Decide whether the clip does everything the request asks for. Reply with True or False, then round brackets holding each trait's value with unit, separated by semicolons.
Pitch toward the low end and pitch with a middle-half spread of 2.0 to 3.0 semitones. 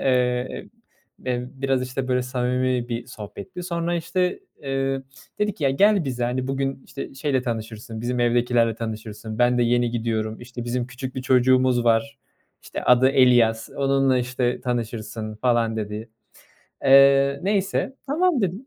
True (125 Hz; 2.4 semitones)